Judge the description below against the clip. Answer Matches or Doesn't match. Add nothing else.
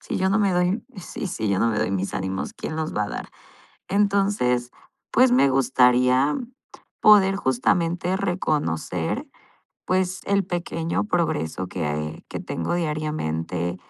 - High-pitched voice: Doesn't match